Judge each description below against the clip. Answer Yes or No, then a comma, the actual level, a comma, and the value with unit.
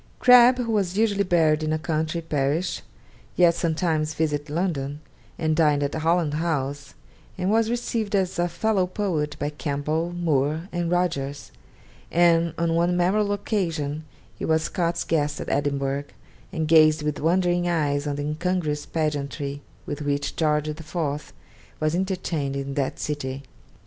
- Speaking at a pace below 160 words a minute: Yes, average, 150 wpm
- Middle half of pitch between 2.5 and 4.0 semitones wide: Yes, average, 3.2 semitones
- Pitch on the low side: No, medium, 160 Hz